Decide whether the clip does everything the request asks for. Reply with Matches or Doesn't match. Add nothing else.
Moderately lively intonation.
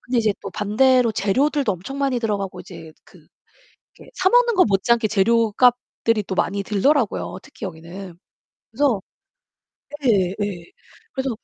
Matches